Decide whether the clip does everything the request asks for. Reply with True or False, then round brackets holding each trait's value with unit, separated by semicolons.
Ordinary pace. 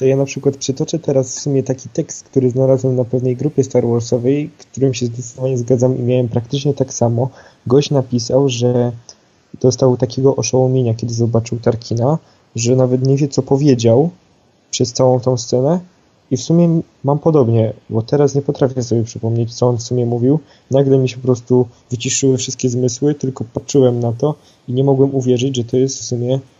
False (185 wpm)